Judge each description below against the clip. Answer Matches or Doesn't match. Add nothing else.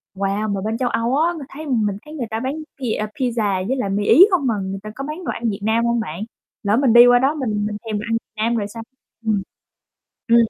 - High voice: Matches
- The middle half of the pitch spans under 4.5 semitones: Matches